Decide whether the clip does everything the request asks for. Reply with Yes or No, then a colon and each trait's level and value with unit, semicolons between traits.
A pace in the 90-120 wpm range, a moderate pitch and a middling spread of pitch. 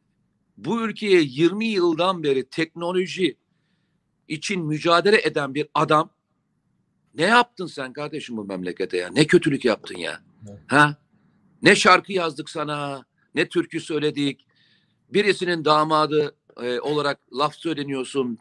Yes: average, 115 wpm; medium, 155 Hz; average, 3.6 semitones